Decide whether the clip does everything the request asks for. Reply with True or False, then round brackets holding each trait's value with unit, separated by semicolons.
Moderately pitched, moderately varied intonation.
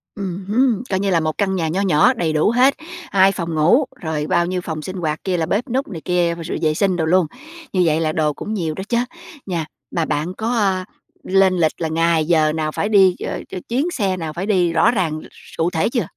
True (180 Hz; 3.7 semitones)